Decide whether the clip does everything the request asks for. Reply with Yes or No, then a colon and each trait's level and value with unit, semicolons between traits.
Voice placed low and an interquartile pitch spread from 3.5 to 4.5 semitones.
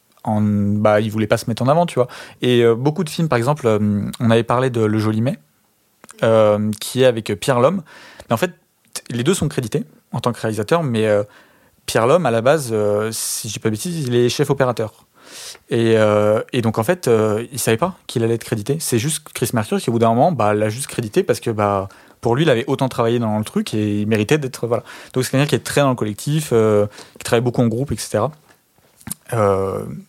Yes: low, 115 Hz; average, 3.8 semitones